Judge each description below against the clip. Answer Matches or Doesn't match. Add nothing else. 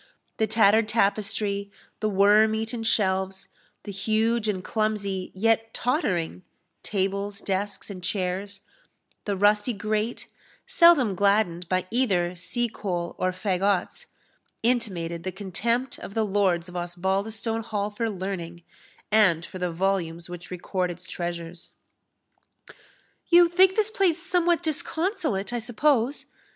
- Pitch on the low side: Doesn't match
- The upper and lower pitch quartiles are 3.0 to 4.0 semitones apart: Matches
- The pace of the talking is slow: Matches